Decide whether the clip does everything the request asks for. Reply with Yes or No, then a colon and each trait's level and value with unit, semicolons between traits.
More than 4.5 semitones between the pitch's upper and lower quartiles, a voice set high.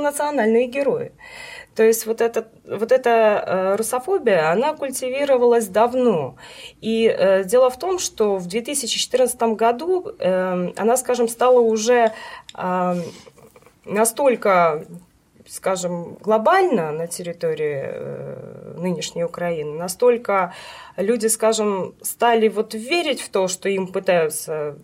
Yes: wide, 5.4 semitones; high, 225 Hz